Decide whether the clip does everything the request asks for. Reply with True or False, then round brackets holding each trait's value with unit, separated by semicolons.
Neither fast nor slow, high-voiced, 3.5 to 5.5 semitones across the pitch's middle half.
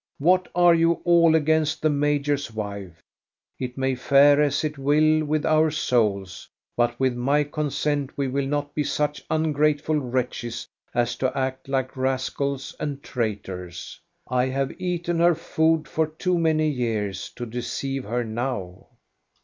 False (150 wpm; 140 Hz; 3.9 semitones)